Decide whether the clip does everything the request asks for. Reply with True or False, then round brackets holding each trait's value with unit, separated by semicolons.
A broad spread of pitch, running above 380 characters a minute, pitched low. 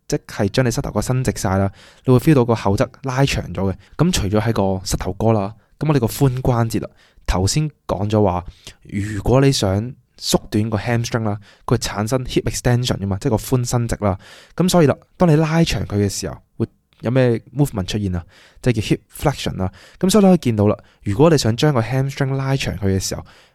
False (4.9 semitones; 400 characters per minute; 115 Hz)